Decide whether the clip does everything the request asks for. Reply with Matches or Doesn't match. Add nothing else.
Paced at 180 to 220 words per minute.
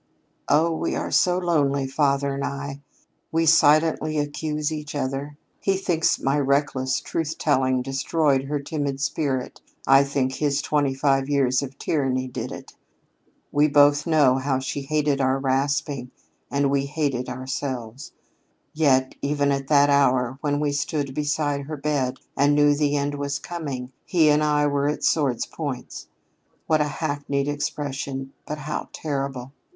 Doesn't match